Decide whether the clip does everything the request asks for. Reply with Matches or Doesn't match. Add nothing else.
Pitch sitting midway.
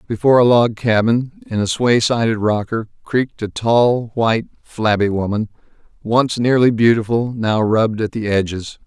Doesn't match